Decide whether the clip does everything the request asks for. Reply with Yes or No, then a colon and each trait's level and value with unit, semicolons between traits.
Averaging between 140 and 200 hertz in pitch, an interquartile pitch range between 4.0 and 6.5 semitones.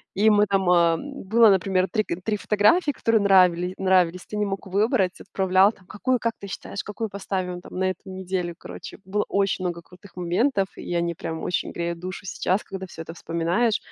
No: high, 190 Hz; narrow, 2.5 semitones